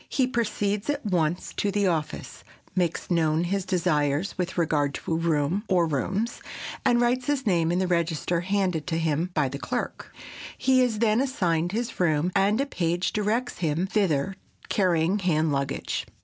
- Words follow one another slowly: No, average, 175 wpm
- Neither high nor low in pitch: Yes, medium, 180 Hz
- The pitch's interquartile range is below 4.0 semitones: No, average, 4.4 semitones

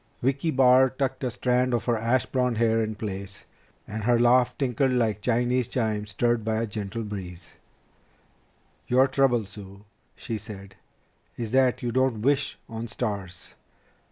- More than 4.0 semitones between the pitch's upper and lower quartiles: No, average, 3.2 semitones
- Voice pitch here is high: No, low, 115 Hz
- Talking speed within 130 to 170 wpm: Yes, average, 155 wpm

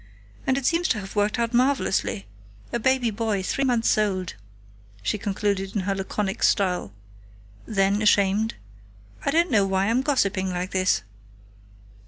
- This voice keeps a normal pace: Yes, average, 150 wpm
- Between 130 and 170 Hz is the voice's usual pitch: No, high, 205 Hz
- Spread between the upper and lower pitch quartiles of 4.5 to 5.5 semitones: No, average, 3.6 semitones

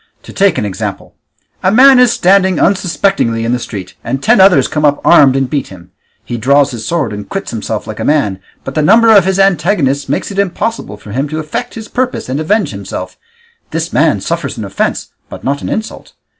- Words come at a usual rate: No, fast, 210 wpm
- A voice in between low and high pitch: Yes, medium, 155 Hz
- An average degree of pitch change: No, wide, 7.9 semitones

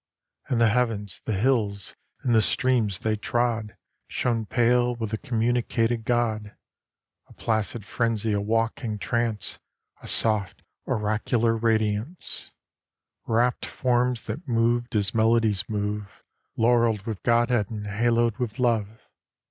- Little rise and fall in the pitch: Yes, narrow, 2.0 semitones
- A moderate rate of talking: No, slow, 125 wpm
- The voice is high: No, low, 115 Hz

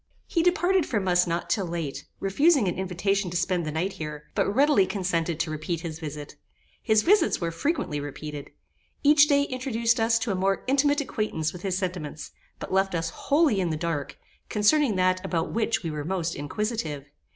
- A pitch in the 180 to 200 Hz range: Yes, medium, 185 Hz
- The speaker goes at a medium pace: Yes, average, 185 wpm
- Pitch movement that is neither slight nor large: No, wide, 5.9 semitones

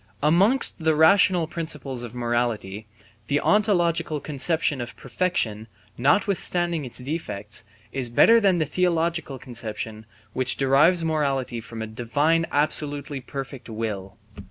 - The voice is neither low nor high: Yes, medium, 145 Hz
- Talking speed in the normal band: No, slow, 120 wpm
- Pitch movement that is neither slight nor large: No, wide, 5.7 semitones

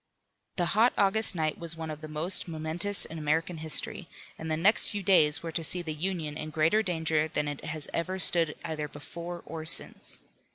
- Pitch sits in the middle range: Yes, medium, 160 Hz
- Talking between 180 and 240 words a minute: Yes, average, 200 wpm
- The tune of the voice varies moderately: No, narrow, 2.3 semitones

